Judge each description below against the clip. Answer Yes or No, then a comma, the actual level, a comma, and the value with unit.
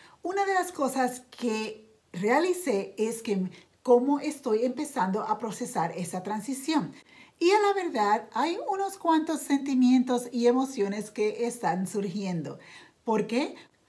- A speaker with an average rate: No, slow, 130 wpm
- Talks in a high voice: Yes, high, 245 Hz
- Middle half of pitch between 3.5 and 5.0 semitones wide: No, wide, 5.5 semitones